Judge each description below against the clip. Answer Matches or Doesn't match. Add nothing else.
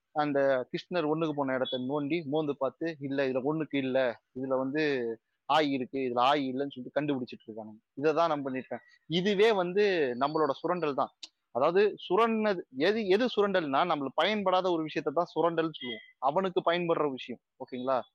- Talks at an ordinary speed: Doesn't match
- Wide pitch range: Doesn't match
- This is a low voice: Doesn't match